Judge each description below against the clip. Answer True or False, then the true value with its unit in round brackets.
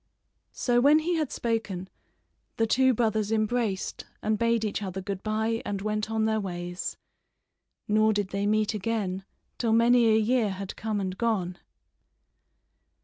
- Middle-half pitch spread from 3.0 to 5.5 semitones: False (2.5 semitones)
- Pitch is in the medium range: False (215 Hz)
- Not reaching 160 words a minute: True (150 wpm)